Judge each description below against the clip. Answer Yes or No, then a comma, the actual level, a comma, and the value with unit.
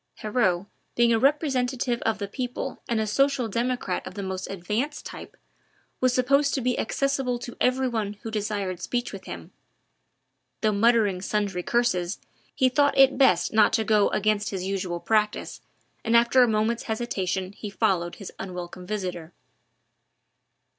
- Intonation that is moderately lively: Yes, average, 4.3 semitones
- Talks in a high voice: Yes, high, 220 Hz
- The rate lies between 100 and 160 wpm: Yes, average, 155 wpm